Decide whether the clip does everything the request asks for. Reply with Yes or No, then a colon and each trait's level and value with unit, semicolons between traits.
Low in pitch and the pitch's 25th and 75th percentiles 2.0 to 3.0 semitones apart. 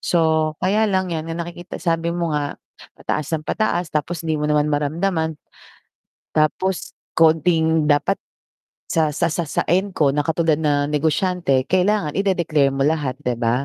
No: medium, 160 Hz; average, 2.7 semitones